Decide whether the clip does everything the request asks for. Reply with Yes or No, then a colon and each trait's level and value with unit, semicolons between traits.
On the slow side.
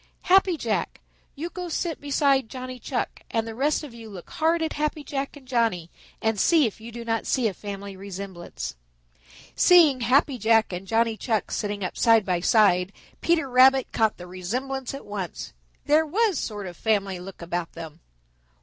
No: average, 180 wpm